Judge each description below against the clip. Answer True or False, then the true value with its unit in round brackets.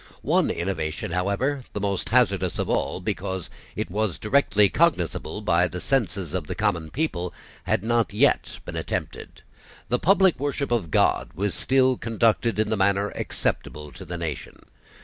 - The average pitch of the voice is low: True (100 Hz)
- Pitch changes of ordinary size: True (4.9 semitones)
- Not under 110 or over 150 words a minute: False (160 wpm)